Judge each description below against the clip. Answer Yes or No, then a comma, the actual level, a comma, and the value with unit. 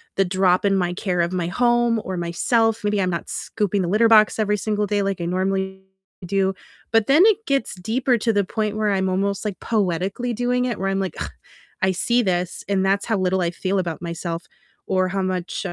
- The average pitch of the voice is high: Yes, high, 195 Hz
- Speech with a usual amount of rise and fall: Yes, average, 3.0 semitones